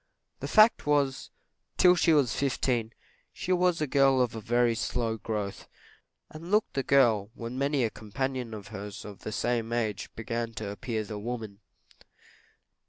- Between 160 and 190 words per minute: Yes, average, 165 wpm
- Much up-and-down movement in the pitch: No, average, 3.9 semitones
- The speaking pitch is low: Yes, low, 120 Hz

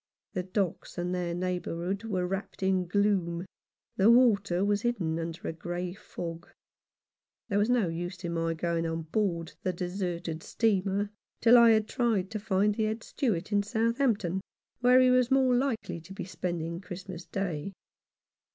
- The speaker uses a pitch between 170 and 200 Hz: Yes, high, 190 Hz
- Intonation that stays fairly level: No, average, 3.7 semitones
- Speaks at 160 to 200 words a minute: Yes, average, 165 wpm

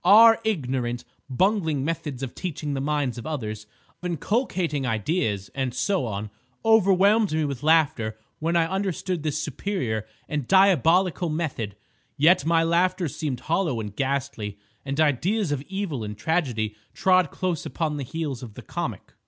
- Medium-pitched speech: Yes, medium, 155 Hz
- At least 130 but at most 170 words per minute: Yes, average, 155 wpm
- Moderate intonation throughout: No, wide, 6.1 semitones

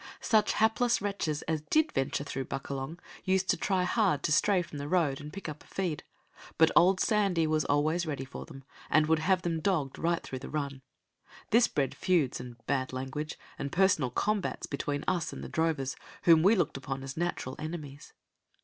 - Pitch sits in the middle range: Yes, medium, 160 Hz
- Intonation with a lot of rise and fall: No, average, 4.8 semitones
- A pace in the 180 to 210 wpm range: Yes, average, 195 wpm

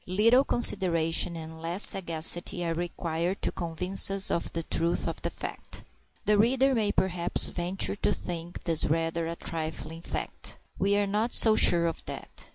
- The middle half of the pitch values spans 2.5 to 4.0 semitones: Yes, average, 3.3 semitones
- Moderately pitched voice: Yes, medium, 175 Hz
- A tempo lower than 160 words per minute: No, average, 165 wpm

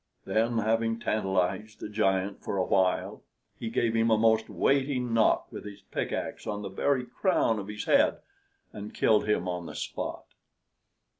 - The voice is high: No, low, 110 Hz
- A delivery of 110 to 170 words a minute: Yes, average, 165 wpm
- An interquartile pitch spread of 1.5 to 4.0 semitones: Yes, narrow, 2.4 semitones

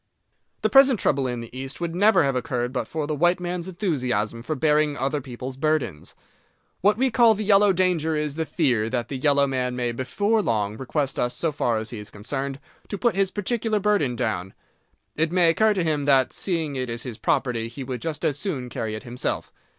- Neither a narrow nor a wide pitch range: No, wide, 6.1 semitones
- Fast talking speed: Yes, fast, 210 wpm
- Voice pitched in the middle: Yes, medium, 145 Hz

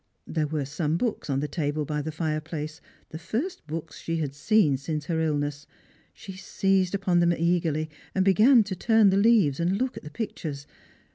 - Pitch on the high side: No, medium, 165 Hz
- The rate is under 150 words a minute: No, average, 190 wpm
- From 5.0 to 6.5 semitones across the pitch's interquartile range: No, average, 4.3 semitones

